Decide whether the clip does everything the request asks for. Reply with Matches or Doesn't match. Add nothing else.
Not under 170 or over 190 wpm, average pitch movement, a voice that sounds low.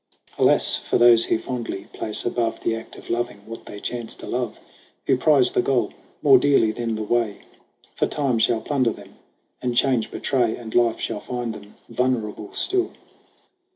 Doesn't match